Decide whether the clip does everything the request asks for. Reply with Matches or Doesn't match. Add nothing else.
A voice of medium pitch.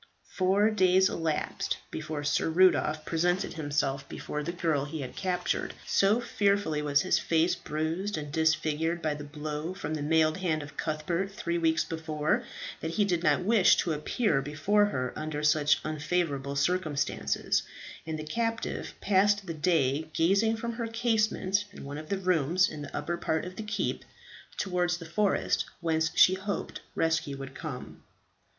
Matches